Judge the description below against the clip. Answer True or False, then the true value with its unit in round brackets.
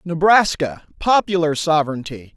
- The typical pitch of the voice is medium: True (165 Hz)